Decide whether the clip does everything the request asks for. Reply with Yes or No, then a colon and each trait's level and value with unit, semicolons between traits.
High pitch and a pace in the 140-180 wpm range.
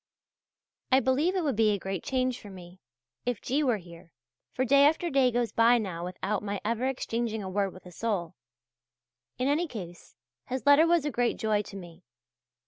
No: high, 230 Hz; average, 195 wpm